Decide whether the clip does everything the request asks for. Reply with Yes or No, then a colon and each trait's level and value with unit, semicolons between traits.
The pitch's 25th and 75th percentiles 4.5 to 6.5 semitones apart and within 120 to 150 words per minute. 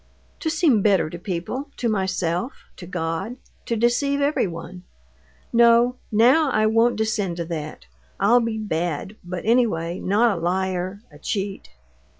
Yes: average, 5.0 semitones; average, 145 wpm